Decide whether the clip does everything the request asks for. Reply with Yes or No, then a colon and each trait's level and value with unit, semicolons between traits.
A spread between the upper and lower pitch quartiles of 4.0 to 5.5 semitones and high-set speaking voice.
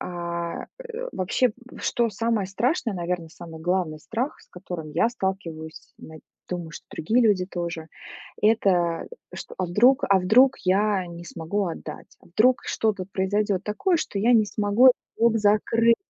Yes: average, 4.6 semitones; high, 195 Hz